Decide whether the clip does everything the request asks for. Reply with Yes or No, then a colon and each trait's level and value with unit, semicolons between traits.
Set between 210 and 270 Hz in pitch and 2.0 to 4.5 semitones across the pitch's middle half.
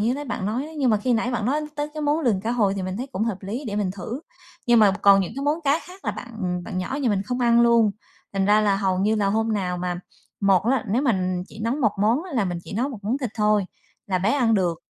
Yes: high, 220 Hz; average, 4.2 semitones